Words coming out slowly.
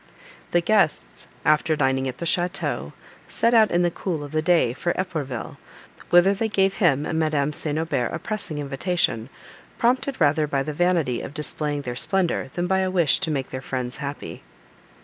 No: average, 185 wpm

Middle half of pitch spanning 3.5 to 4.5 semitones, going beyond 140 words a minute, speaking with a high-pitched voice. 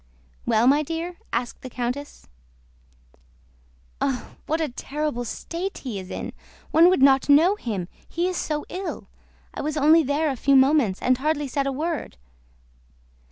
Yes: average, 3.8 semitones; average, 160 wpm; very high, 285 Hz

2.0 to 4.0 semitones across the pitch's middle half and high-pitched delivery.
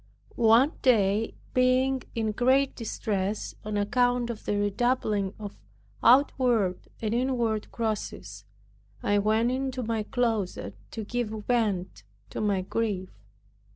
Yes: average, 3.3 semitones; high, 225 Hz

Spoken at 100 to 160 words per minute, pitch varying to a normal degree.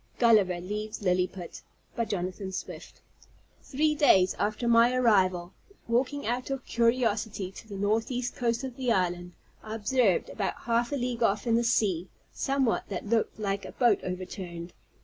Yes: average, 155 wpm; average, 4.2 semitones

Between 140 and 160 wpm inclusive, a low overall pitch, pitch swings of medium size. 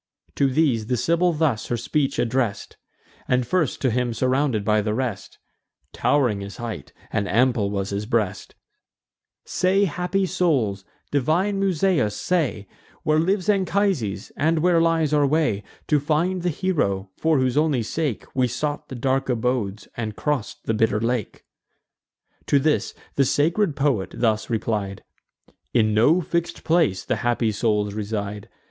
No: average, 150 wpm; low, 130 Hz; wide, 6.8 semitones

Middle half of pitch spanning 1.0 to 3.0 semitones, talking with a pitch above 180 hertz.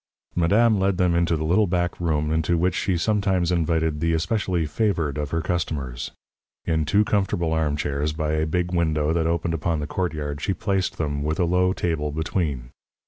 No: average, 2.7 semitones; very low, 85 Hz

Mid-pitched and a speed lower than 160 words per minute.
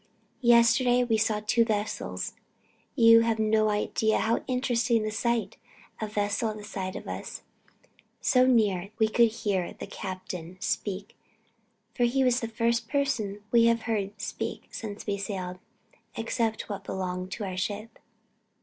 No: high, 220 Hz; average, 150 wpm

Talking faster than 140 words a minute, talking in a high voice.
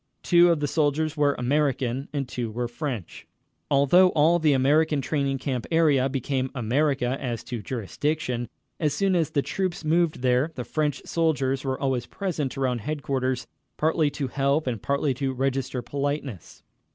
No: average, 160 wpm; medium, 140 Hz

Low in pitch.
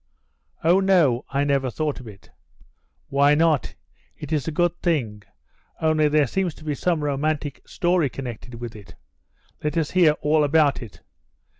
No: medium, 150 Hz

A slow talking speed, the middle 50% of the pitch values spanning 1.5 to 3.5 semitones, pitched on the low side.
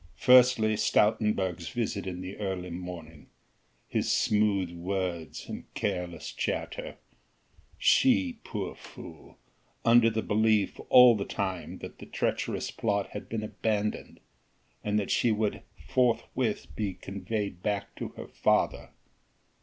Yes: slow, 120 wpm; average, 3.0 semitones; low, 105 Hz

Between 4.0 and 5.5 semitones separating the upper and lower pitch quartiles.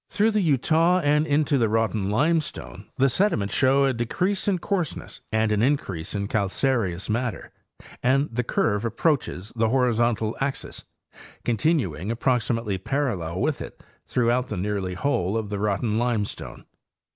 Yes: average, 5.2 semitones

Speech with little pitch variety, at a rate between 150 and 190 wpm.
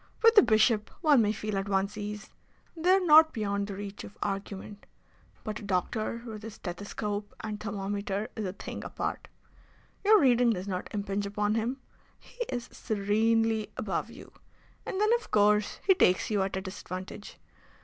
Yes: narrow, 2.2 semitones; average, 170 wpm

